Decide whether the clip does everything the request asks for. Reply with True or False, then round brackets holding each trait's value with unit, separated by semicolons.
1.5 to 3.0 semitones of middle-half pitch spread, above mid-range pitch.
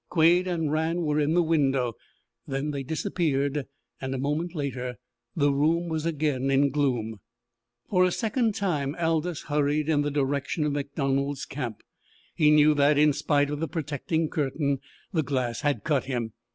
False (2.6 semitones; 145 Hz)